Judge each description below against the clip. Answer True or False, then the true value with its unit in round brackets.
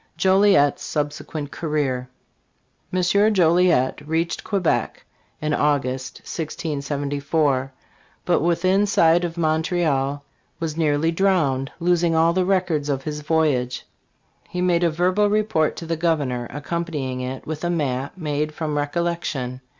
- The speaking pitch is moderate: True (160 Hz)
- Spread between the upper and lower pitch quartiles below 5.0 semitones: True (3.3 semitones)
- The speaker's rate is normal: False (125 wpm)